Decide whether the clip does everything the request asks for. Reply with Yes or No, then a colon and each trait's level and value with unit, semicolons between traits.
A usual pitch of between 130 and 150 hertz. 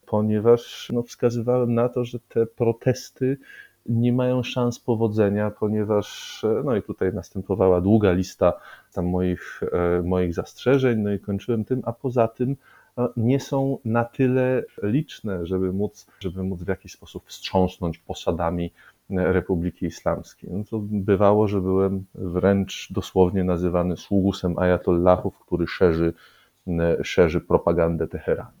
No: low, 100 Hz